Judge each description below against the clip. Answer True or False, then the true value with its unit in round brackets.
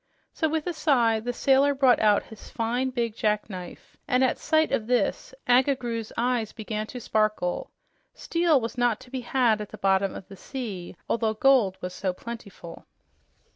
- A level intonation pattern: False (3.5 semitones)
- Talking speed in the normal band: True (175 wpm)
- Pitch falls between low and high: False (235 Hz)